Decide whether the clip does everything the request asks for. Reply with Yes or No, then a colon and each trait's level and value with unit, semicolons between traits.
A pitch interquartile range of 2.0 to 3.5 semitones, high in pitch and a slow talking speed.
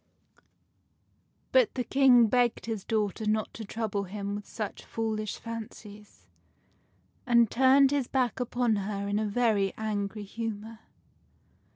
Yes: narrow, 2.6 semitones; high, 220 Hz; slow, 130 wpm